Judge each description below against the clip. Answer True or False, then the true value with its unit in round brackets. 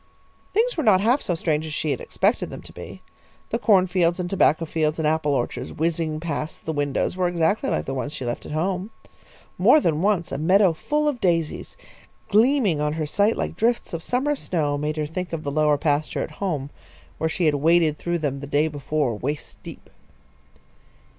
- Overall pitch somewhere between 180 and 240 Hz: False (160 Hz)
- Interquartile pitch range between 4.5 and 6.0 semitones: False (3.8 semitones)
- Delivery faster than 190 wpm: True (205 wpm)